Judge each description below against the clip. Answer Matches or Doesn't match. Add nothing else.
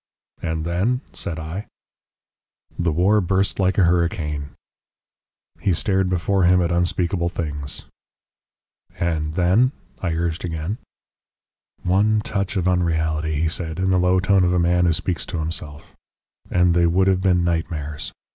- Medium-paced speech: Matches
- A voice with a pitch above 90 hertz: Doesn't match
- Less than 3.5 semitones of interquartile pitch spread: Matches